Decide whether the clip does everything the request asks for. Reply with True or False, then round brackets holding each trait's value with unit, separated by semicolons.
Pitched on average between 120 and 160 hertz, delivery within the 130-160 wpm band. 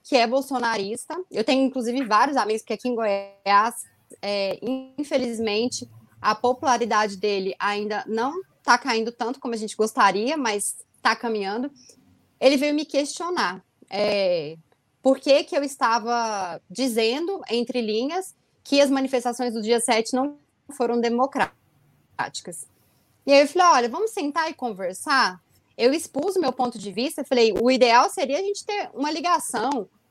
False (245 Hz; 155 wpm)